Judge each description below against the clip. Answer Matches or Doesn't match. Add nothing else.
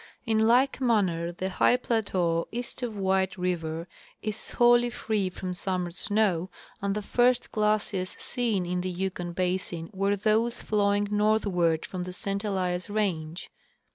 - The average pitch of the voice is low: Doesn't match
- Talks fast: Doesn't match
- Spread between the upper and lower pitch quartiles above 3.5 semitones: Doesn't match